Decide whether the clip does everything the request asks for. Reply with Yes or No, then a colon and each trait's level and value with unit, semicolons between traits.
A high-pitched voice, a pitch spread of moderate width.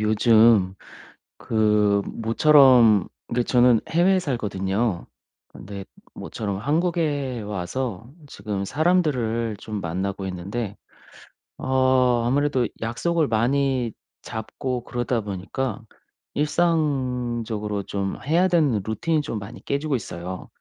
No: low, 120 Hz; average, 5.0 semitones